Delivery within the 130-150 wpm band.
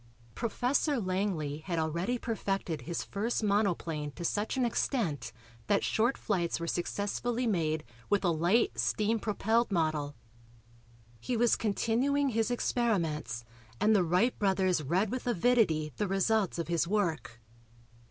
Yes: slow, 135 wpm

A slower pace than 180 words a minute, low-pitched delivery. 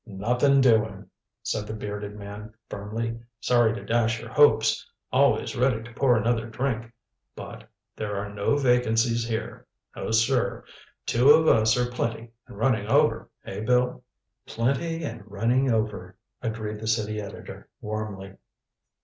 Yes: average, 140 wpm; low, 115 Hz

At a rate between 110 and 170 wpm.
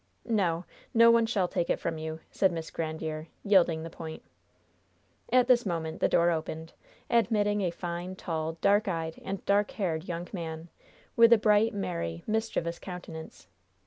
Yes: average, 160 wpm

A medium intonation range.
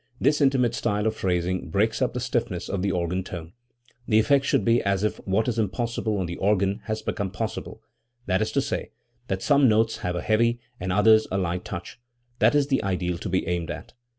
Yes: average, 4.0 semitones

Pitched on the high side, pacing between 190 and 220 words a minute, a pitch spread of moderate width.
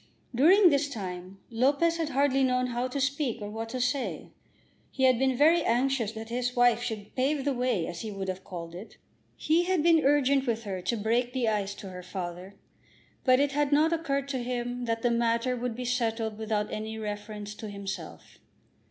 Yes: high, 245 Hz; average, 200 wpm; average, 4.2 semitones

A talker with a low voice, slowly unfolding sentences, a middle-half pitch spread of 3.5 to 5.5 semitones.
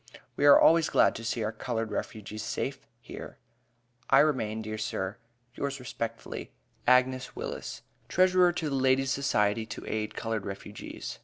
No: low, 115 Hz; average, 150 wpm; average, 4.0 semitones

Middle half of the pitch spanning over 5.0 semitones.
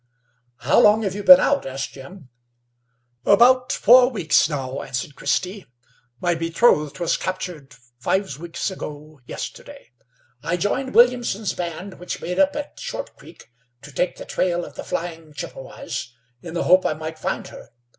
Yes: wide, 5.5 semitones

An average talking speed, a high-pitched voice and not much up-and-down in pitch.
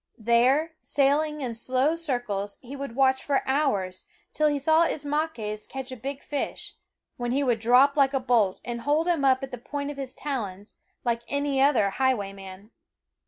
No: average, 180 wpm; very high, 265 Hz; average, 3.5 semitones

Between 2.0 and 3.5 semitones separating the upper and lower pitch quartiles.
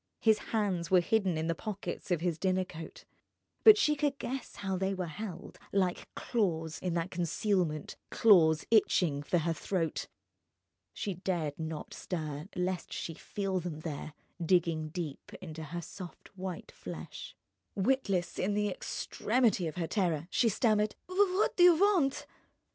No: average, 4.3 semitones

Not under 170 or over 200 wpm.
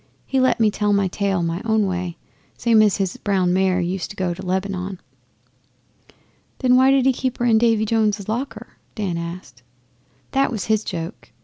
Yes: average, 185 wpm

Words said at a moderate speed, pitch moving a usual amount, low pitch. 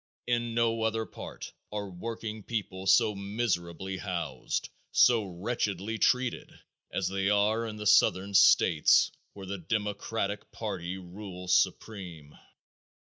No: slow, 120 wpm; average, 3.1 semitones; low, 100 Hz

